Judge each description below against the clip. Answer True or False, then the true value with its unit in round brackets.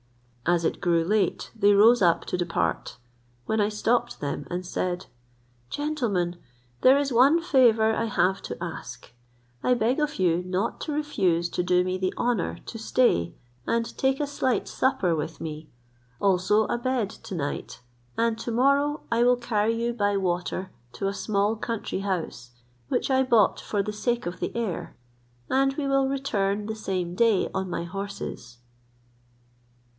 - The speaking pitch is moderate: False (210 Hz)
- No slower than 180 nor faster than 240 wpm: False (165 wpm)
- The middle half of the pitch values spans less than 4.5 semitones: False (5.1 semitones)